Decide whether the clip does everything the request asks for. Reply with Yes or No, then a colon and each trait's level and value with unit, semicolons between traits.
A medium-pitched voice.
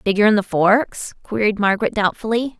No: high, 210 Hz